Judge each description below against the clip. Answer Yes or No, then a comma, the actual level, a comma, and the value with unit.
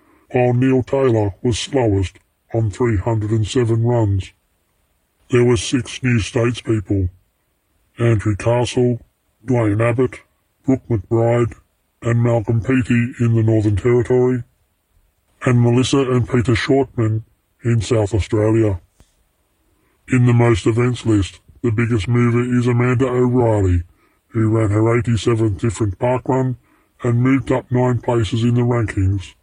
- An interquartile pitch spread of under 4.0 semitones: Yes, average, 2.9 semitones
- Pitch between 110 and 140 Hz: Yes, low, 115 Hz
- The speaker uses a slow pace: Yes, slow, 120 wpm